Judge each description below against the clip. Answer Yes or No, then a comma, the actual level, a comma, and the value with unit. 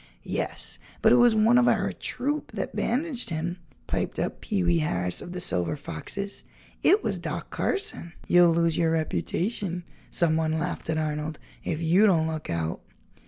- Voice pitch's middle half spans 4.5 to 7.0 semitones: Yes, average, 4.8 semitones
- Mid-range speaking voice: Yes, medium, 170 Hz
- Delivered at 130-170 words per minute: Yes, average, 165 wpm